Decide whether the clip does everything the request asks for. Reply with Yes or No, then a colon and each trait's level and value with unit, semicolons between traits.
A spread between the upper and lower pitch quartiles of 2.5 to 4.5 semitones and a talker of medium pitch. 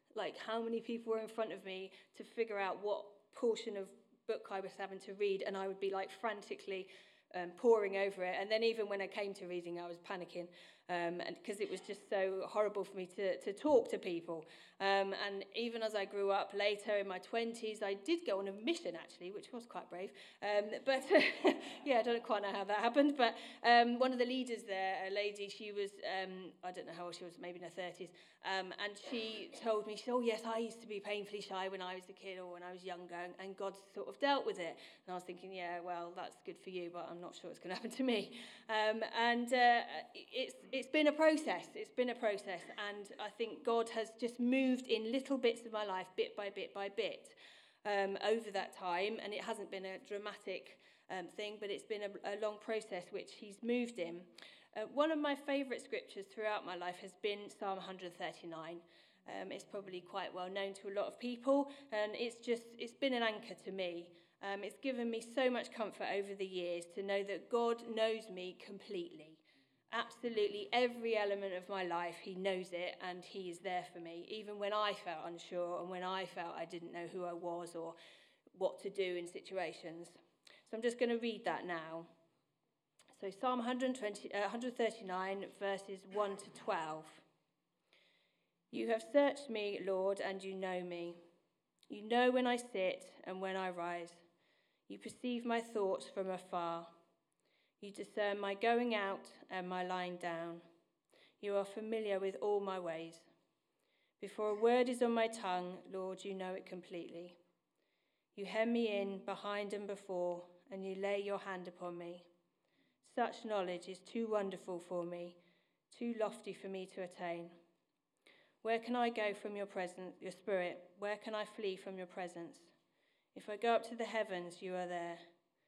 No: average, 3.8 semitones; high, 200 Hz